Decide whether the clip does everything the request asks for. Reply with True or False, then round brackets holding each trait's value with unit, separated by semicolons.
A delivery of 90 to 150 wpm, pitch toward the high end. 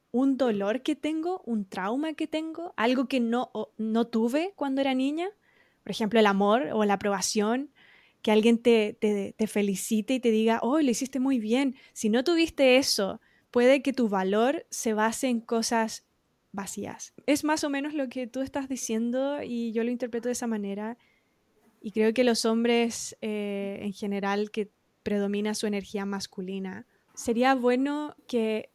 False (175 wpm; 235 Hz)